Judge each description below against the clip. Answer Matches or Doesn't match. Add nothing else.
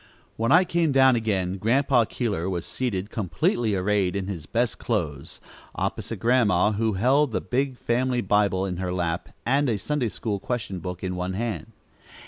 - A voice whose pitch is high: Doesn't match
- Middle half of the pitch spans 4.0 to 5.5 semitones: Matches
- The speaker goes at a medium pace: Matches